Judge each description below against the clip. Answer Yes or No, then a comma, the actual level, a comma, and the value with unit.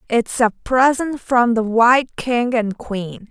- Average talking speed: Yes, average, 165 wpm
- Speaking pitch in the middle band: No, high, 235 Hz